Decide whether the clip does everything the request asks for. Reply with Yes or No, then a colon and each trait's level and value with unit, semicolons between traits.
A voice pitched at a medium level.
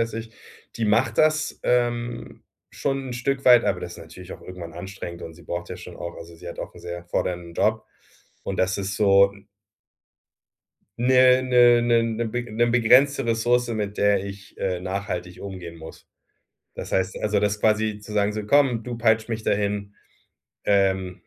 No: low, 105 Hz